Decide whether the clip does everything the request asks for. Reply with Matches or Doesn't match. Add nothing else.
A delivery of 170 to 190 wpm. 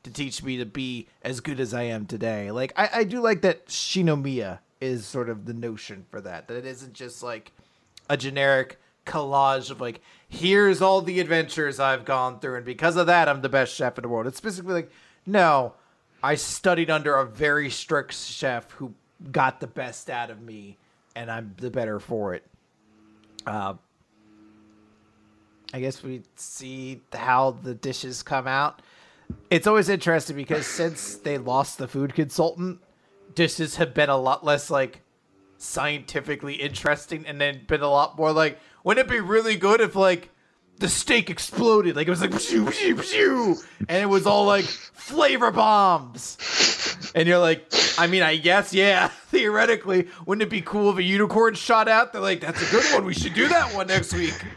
Matches